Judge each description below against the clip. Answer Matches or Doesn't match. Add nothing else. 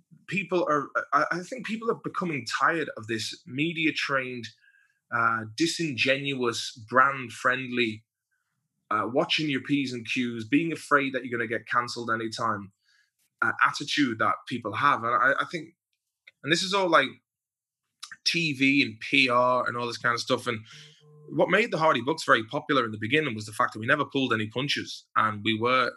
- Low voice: Matches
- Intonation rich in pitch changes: Doesn't match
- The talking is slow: Doesn't match